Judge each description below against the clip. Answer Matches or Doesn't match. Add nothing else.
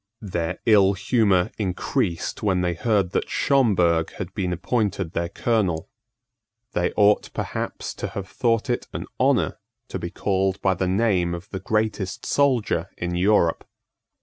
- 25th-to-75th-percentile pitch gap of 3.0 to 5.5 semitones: Matches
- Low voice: Matches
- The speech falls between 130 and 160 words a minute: Matches